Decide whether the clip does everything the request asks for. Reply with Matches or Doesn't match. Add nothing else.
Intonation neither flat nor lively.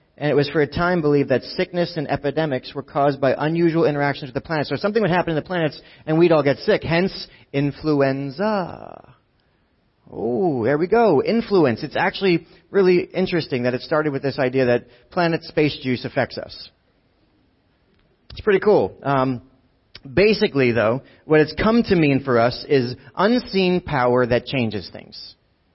Matches